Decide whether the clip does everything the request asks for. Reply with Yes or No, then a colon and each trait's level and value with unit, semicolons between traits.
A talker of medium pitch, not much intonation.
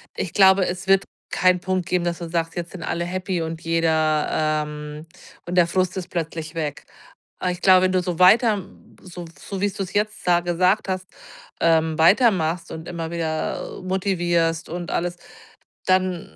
Yes: medium, 175 Hz; narrow, 2.2 semitones